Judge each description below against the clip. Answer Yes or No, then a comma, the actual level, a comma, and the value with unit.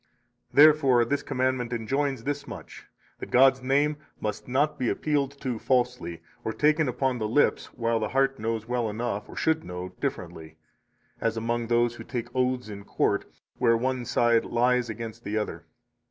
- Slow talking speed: No, average, 170 wpm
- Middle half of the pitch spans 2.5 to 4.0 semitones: Yes, average, 3.0 semitones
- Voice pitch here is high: No, low, 120 Hz